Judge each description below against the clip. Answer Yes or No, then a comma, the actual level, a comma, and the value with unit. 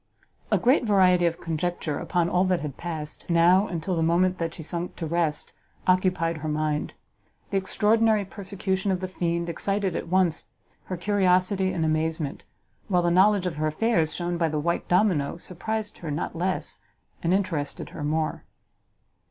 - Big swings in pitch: No, narrow, 2.6 semitones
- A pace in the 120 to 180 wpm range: Yes, average, 170 wpm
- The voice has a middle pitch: Yes, medium, 175 Hz